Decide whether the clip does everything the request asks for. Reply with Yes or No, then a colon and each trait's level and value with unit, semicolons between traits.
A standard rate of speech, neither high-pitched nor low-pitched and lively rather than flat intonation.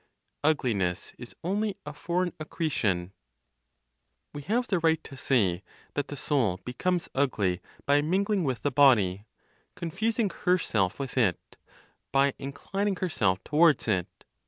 No: slow, 130 wpm; medium, 145 Hz; wide, 8.1 semitones